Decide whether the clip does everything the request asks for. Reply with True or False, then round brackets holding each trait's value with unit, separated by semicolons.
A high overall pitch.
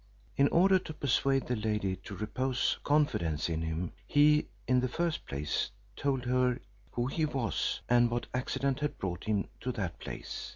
False (125 Hz)